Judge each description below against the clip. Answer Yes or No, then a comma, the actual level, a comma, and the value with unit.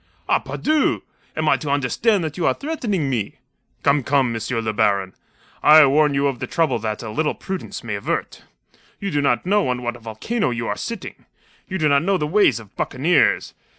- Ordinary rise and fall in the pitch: No, wide, 7.0 semitones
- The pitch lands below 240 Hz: Yes, medium, 140 Hz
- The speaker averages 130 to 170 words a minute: No, fast, 205 wpm